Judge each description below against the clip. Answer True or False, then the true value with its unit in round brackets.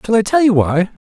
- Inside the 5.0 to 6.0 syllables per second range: True (5.6 syllables/s)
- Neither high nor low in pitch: True (180 Hz)